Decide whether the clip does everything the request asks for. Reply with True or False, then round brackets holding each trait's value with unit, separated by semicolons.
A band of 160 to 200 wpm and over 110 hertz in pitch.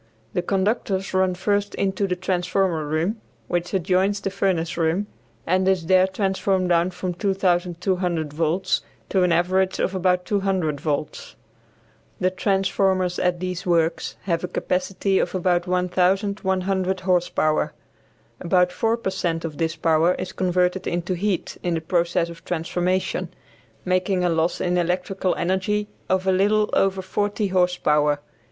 False (145 wpm; 185 Hz)